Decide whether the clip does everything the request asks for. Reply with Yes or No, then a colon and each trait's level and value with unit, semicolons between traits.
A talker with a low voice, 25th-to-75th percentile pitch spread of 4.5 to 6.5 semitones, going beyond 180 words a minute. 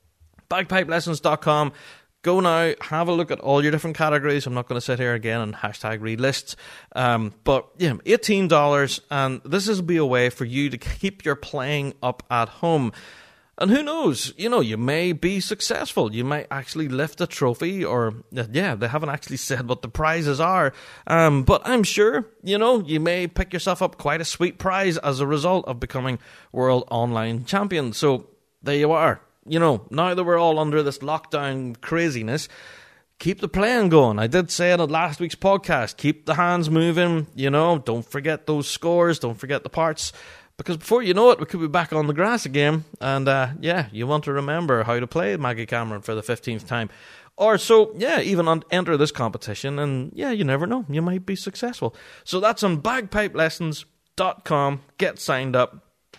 No: medium, 155 Hz; average, 5.2 semitones; average, 195 wpm